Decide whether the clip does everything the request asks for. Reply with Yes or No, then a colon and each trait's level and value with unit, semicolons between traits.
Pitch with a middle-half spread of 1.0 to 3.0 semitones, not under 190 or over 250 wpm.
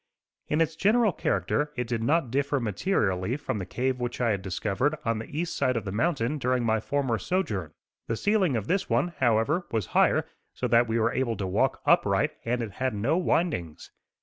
No: average, 5.2 semitones; average, 200 wpm